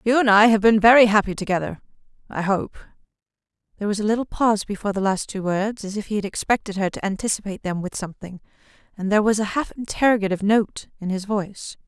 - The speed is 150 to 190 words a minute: No, average, 200 wpm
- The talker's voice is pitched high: Yes, high, 205 Hz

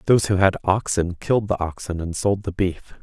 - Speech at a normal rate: No, fast, 220 wpm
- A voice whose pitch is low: Yes, very low, 95 Hz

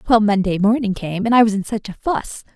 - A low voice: No, high, 210 Hz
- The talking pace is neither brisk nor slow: No, fast, 260 wpm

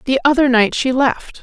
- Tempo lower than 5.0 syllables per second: Yes, 4.8 syllables/s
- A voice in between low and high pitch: No, very high, 260 Hz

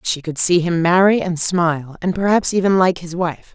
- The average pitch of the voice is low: No, medium, 175 Hz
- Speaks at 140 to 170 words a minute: No, fast, 205 wpm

